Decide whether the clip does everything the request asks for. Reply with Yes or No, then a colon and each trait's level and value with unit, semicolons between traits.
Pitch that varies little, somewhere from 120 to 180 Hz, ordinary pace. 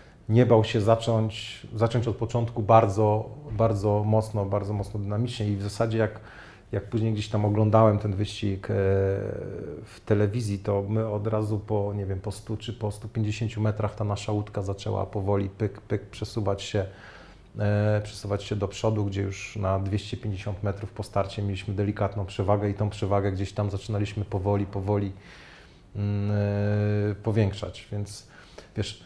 No: narrow, 1.4 semitones; low, 105 Hz; average, 150 wpm